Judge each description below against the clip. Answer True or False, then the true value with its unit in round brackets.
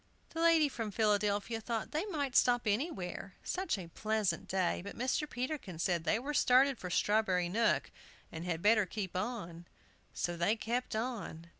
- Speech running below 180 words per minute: True (165 wpm)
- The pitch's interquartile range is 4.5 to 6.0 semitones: True (5.4 semitones)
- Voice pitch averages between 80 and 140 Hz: False (215 Hz)